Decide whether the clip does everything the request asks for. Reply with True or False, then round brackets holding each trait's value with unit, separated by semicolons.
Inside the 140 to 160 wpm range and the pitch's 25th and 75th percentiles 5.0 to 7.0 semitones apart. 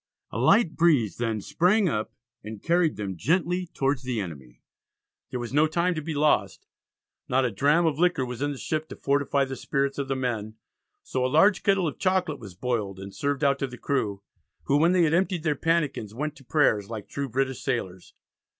False (205 wpm; 5.5 semitones)